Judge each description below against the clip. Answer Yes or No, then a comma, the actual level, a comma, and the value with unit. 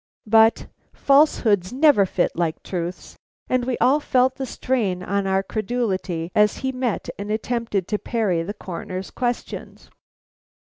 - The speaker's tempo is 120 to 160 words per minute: Yes, average, 140 wpm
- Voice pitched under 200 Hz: No, high, 215 Hz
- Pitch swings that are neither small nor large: Yes, average, 5.0 semitones